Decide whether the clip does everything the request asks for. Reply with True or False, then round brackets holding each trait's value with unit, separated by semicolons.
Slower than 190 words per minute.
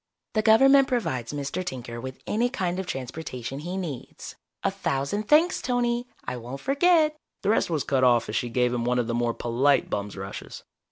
False (200 wpm)